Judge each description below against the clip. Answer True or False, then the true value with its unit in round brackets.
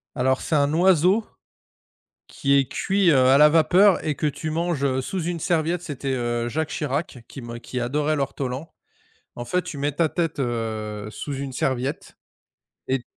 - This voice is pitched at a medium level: True (145 Hz)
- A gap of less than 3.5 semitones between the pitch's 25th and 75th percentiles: False (4.2 semitones)